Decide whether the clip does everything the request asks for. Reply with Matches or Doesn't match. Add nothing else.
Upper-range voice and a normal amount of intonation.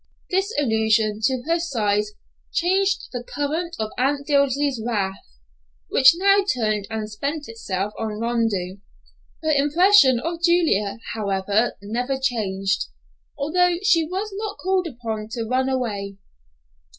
Doesn't match